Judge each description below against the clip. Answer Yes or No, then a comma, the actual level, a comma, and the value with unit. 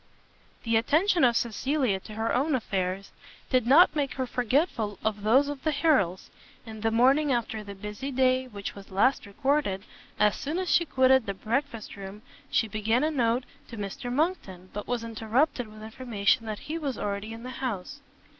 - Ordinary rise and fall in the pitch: Yes, average, 4.5 semitones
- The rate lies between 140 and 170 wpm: No, average, 185 wpm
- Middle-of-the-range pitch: No, high, 235 Hz